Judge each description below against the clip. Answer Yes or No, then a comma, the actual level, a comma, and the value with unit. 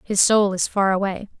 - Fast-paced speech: Yes, fast, 215 wpm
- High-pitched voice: Yes, high, 200 Hz